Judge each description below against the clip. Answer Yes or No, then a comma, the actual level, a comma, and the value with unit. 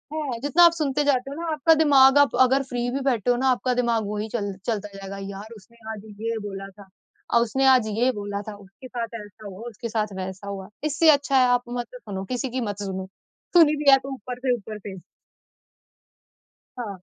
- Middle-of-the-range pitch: No, high, 235 Hz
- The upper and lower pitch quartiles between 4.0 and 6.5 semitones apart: Yes, average, 4.5 semitones